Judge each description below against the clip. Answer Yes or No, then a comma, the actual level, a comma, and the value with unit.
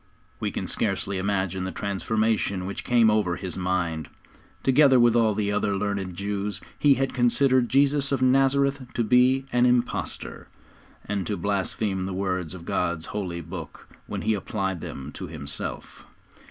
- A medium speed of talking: Yes, average, 155 wpm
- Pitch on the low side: Yes, low, 100 Hz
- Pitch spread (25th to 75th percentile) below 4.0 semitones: No, average, 4.8 semitones